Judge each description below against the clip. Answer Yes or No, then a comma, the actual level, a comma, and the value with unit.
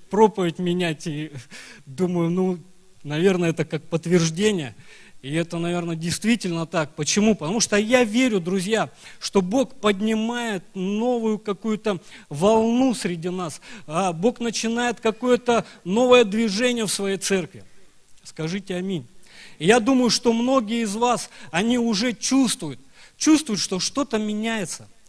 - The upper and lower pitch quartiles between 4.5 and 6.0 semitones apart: Yes, average, 4.9 semitones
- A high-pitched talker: Yes, high, 205 Hz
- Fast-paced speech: No, average, 125 wpm